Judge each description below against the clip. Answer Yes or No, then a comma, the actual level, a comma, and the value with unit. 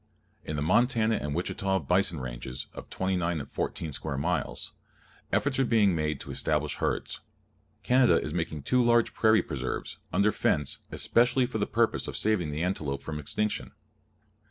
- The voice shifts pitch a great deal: Yes, wide, 6.6 semitones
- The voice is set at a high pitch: No, very low, 90 Hz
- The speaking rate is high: No, average, 160 wpm